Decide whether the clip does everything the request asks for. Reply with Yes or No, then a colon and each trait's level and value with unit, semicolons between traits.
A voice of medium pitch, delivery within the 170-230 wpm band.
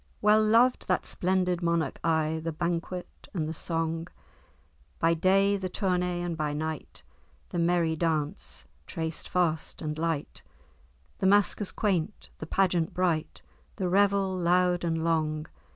No: medium, 170 Hz; slow, 135 wpm